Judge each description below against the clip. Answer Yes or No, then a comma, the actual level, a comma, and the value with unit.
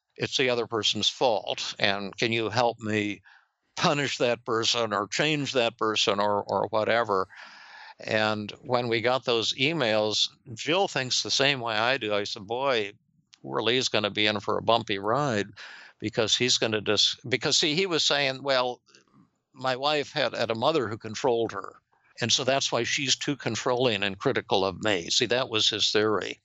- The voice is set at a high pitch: No, low, 115 Hz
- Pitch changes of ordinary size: Yes, average, 3.4 semitones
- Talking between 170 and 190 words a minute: Yes, average, 180 wpm